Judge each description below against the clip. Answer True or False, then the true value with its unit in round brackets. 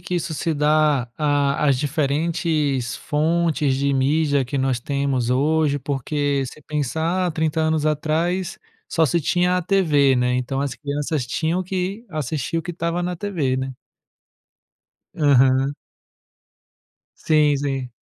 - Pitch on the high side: False (150 Hz)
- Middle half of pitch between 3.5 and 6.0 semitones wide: False (3.1 semitones)